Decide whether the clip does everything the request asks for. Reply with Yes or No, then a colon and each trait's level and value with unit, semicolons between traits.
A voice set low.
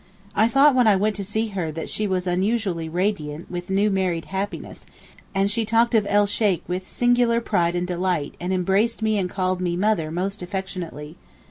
No: high, 190 Hz